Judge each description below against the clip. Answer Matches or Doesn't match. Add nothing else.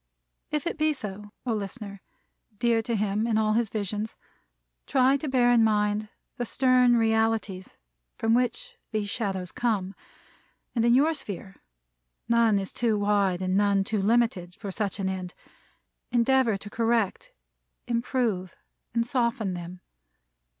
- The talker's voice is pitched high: Matches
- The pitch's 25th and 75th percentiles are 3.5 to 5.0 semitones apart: Doesn't match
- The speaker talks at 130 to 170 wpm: Matches